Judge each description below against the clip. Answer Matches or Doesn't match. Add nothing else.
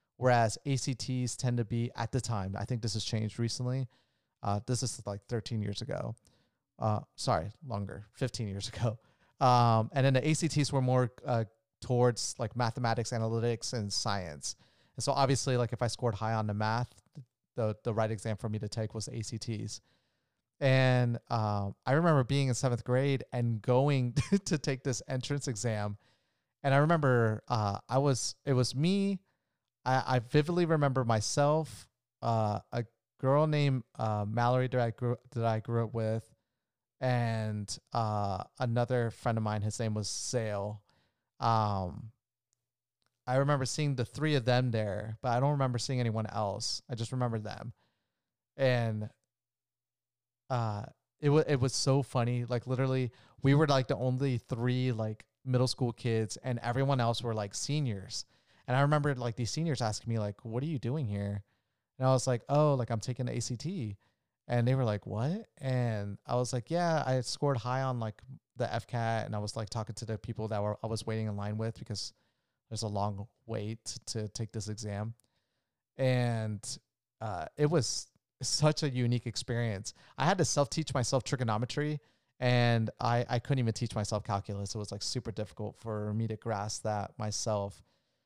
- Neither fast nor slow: Matches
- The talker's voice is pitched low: Matches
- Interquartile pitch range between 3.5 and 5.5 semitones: Doesn't match